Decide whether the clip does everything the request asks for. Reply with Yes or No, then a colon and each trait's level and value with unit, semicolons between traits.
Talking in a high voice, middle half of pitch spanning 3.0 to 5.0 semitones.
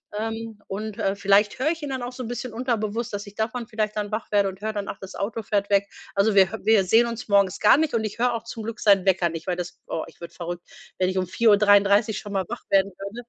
No: high, 210 Hz; narrow, 2.5 semitones